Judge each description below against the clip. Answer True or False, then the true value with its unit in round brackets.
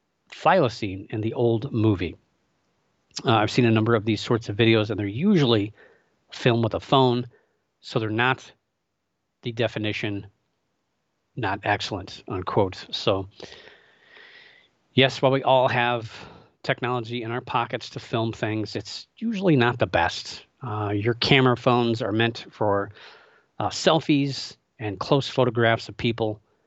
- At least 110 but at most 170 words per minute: True (140 wpm)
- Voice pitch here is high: False (120 Hz)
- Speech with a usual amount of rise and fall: True (3.2 semitones)